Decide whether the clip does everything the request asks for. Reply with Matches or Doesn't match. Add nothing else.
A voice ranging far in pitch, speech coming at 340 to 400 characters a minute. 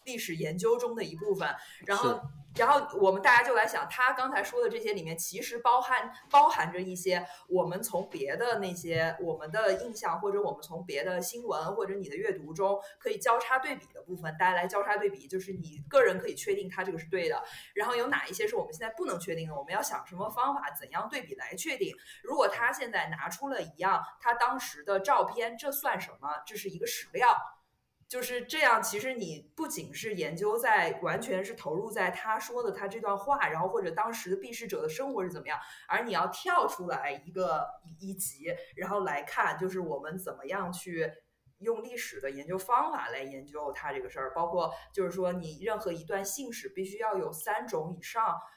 Doesn't match